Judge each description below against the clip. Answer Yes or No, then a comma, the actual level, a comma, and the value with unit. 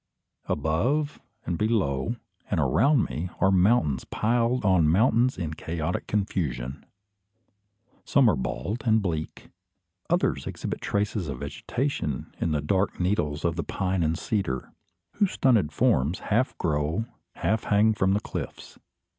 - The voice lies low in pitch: Yes, very low, 95 Hz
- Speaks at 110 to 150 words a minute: Yes, slow, 135 wpm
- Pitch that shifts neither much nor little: No, wide, 6.2 semitones